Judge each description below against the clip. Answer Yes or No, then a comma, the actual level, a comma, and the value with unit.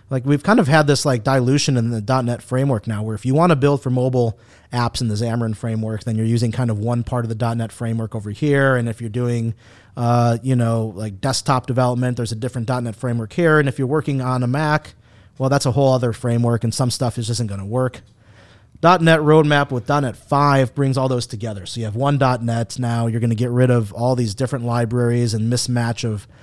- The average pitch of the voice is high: No, low, 120 Hz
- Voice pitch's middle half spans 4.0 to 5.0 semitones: No, narrow, 2.5 semitones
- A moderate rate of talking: No, fast, 240 wpm